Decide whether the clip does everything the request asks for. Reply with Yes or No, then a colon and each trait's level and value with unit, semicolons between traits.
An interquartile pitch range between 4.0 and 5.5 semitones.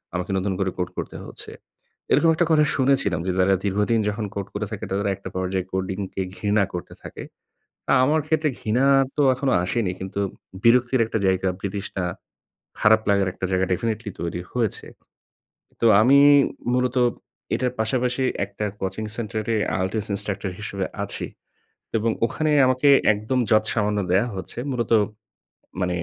Yes: average, 4.3 semitones